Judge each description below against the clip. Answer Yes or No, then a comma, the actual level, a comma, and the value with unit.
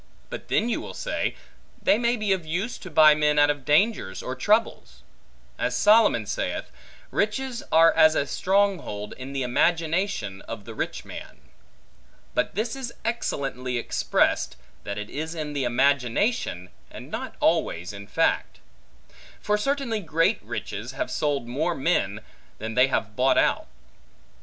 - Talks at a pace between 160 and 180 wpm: No, average, 150 wpm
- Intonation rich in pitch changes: Yes, wide, 8.7 semitones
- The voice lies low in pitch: No, medium, 155 Hz